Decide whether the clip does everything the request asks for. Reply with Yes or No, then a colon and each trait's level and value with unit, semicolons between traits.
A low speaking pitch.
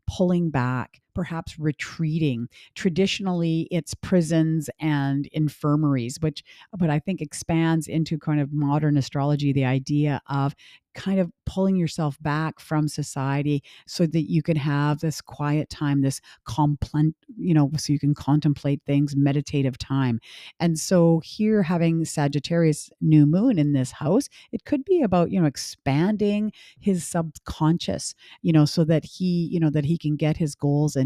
No: medium, 155 Hz